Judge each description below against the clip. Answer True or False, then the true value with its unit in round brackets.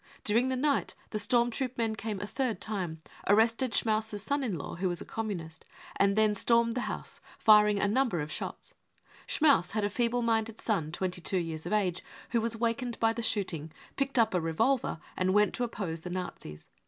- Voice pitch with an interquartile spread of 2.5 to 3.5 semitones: False (4.1 semitones)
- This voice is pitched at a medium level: False (215 Hz)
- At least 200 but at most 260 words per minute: True (205 wpm)